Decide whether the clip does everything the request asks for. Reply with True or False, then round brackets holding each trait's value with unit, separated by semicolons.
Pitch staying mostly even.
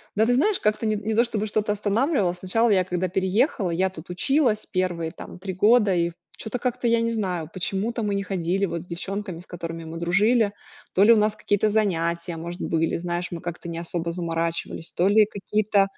False (3.8 semitones)